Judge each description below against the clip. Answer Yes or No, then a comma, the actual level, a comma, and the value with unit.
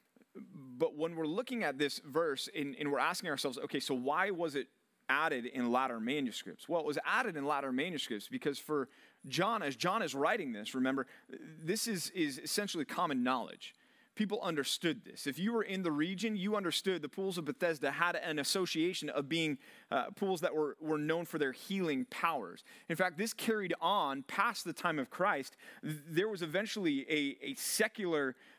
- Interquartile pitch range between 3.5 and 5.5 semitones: Yes, average, 5.2 semitones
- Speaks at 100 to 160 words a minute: No, average, 185 wpm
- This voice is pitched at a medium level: Yes, medium, 165 Hz